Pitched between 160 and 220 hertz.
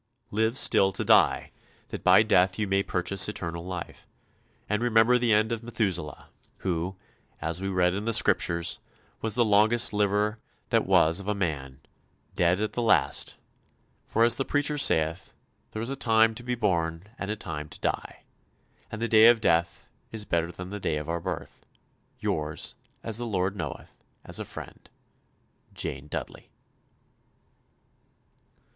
No: low, 100 Hz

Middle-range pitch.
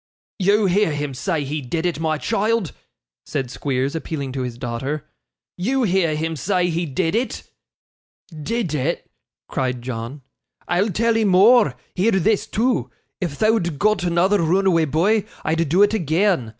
Yes: medium, 170 Hz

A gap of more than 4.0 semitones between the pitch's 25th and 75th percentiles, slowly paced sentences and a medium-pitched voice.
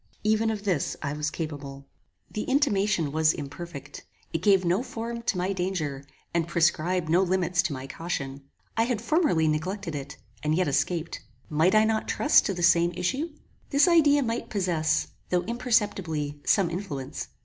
No: wide, 5.6 semitones; average, 165 wpm; medium, 180 Hz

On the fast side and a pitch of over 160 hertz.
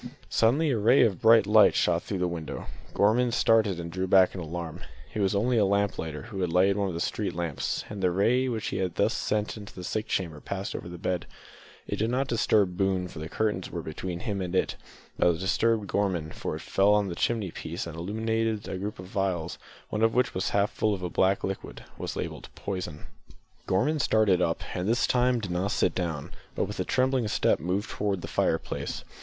No: fast, 220 wpm; low, 100 Hz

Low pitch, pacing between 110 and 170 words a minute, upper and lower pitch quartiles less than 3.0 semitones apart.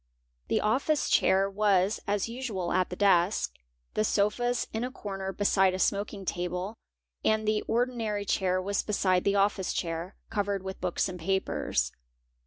No: high, 200 Hz; average, 155 wpm; narrow, 2.4 semitones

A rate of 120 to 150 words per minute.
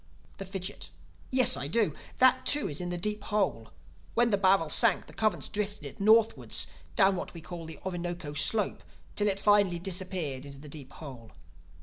No: average, 185 wpm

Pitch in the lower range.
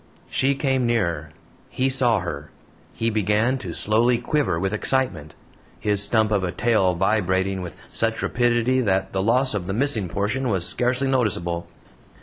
Yes: low, 105 Hz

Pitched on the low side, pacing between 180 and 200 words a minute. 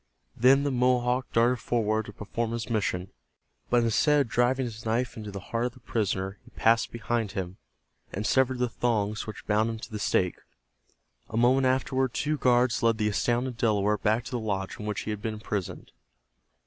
Yes: low, 115 Hz; average, 195 wpm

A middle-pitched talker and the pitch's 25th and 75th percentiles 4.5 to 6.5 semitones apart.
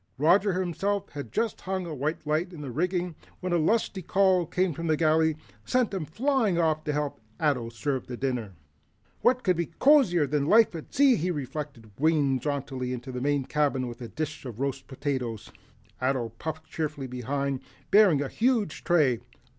Yes: medium, 155 Hz; average, 5.1 semitones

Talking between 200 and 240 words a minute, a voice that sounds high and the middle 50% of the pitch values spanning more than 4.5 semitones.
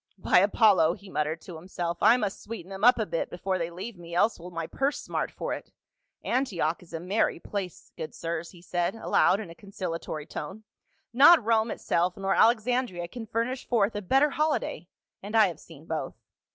Yes: fast, 205 wpm; high, 195 Hz; average, 4.9 semitones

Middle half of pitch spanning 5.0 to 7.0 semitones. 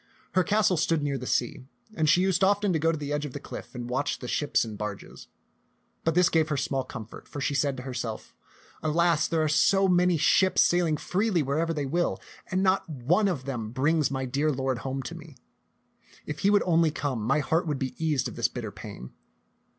No: average, 4.5 semitones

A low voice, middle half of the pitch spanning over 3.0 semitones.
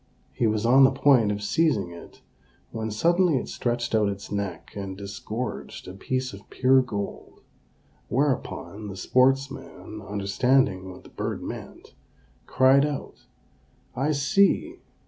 Yes: low, 120 Hz; average, 5.0 semitones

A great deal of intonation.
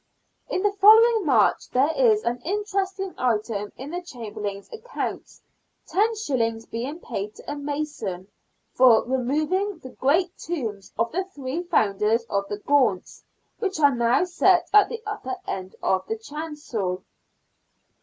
Yes: wide, 8.6 semitones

